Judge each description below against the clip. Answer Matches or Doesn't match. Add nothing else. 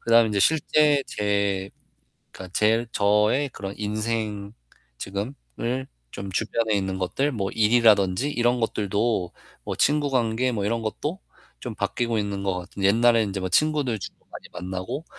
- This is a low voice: Matches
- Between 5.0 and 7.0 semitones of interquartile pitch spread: Doesn't match